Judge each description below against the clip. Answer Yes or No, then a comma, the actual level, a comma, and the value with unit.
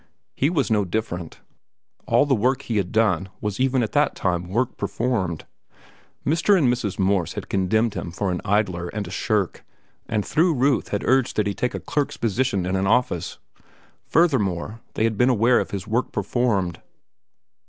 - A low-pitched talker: Yes, low, 110 Hz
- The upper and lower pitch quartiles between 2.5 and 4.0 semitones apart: No, average, 4.8 semitones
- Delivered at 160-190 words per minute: Yes, average, 180 wpm